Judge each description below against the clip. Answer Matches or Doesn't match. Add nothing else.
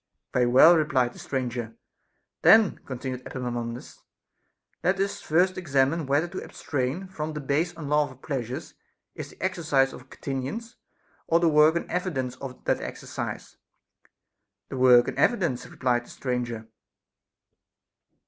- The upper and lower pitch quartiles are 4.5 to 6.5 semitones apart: Matches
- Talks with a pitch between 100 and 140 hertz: Matches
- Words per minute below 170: Matches